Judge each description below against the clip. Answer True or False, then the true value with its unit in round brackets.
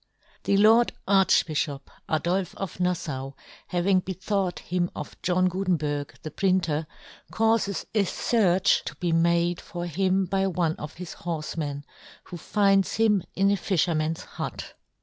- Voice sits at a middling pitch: True (180 Hz)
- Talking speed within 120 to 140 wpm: True (135 wpm)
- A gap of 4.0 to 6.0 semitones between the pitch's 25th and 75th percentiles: False (3.0 semitones)